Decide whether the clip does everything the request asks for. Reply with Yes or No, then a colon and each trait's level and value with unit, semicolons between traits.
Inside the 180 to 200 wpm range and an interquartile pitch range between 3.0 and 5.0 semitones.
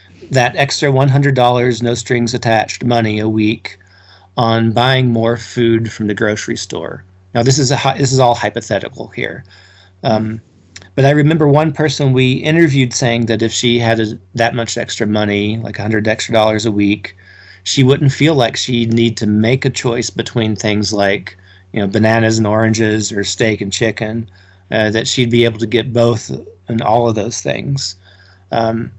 No: average, 185 wpm; narrow, 2.5 semitones